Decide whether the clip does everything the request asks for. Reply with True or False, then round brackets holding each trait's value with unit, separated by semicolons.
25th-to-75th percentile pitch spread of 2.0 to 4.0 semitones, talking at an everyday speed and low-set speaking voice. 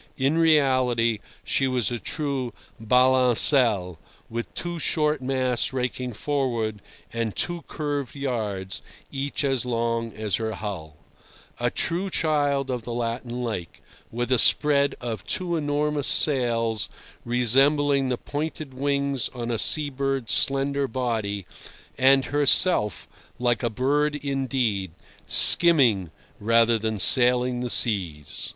False (3.5 semitones; 125 wpm; 125 Hz)